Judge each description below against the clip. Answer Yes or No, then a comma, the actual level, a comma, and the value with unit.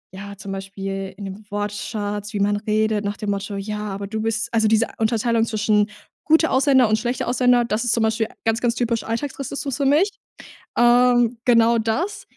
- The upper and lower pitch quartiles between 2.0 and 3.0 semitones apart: Yes, average, 2.7 semitones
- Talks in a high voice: Yes, high, 220 Hz